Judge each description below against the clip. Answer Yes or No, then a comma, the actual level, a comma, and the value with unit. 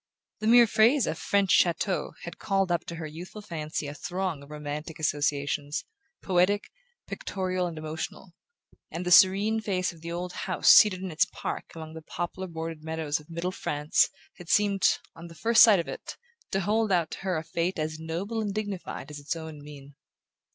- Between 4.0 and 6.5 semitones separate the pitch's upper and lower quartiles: No, average, 3.5 semitones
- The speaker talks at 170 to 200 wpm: Yes, average, 190 wpm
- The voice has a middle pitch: Yes, medium, 170 Hz